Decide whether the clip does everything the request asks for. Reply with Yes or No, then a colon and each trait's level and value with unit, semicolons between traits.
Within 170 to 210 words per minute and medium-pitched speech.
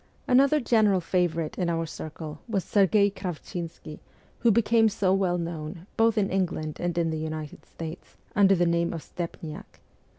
No: average, 160 wpm; medium, 175 Hz